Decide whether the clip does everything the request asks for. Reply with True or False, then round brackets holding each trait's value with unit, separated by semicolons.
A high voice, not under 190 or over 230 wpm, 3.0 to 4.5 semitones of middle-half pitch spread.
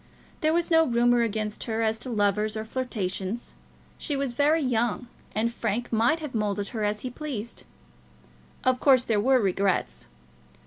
False (230 Hz; 165 wpm; 3.5 semitones)